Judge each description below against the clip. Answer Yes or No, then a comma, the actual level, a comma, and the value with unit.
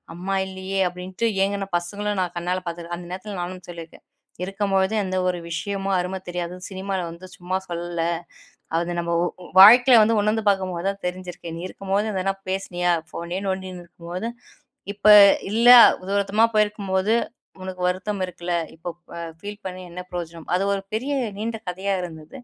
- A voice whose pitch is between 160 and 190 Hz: Yes, medium, 185 Hz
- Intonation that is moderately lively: No, narrow, 2.2 semitones